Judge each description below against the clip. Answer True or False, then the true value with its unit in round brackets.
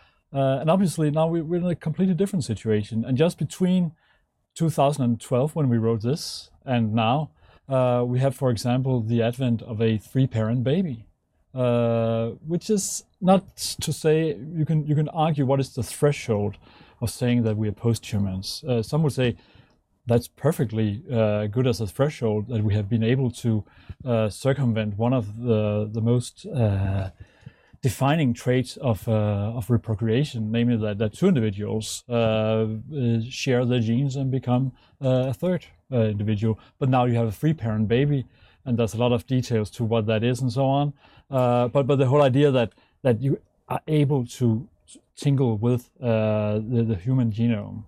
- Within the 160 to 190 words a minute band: True (175 wpm)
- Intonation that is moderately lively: True (3.8 semitones)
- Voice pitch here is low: True (120 Hz)